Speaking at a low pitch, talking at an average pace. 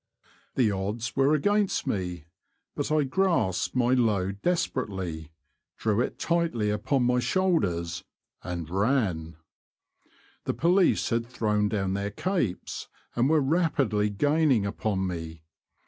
No: low, 110 Hz; slow, 120 wpm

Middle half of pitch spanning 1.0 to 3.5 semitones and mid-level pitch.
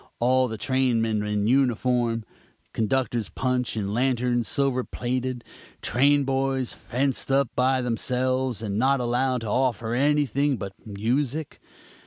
No: narrow, 2.5 semitones; low, 125 Hz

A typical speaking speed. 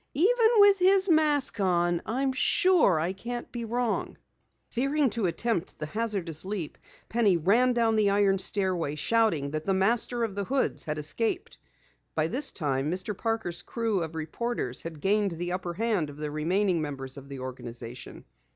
Yes: average, 165 wpm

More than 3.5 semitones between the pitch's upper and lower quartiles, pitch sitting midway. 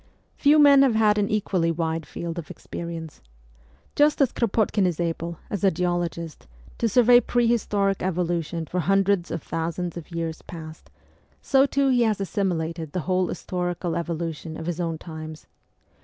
Yes: average, 4.0 semitones; medium, 175 Hz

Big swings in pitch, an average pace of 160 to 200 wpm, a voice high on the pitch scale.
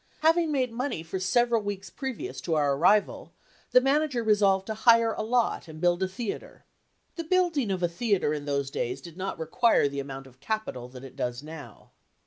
Yes: wide, 7.8 semitones; average, 195 wpm; high, 195 Hz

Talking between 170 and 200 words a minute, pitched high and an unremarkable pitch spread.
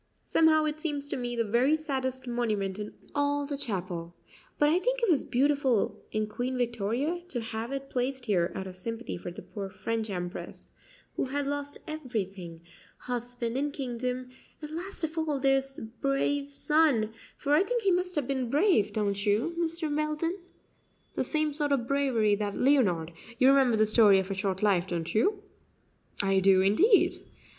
No: average, 175 wpm; very high, 255 Hz; wide, 5.8 semitones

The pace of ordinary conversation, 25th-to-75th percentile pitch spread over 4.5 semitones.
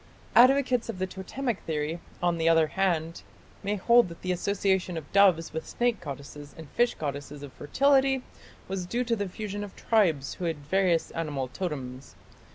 Yes: average, 170 wpm; average, 5.1 semitones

